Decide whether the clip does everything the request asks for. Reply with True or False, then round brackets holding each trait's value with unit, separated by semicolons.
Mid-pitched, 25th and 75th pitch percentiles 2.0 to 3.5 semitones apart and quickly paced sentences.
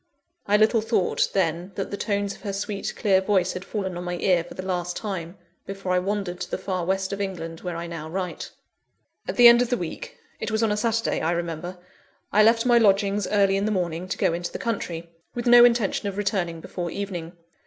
False (195 Hz; 3.0 semitones; 230 wpm)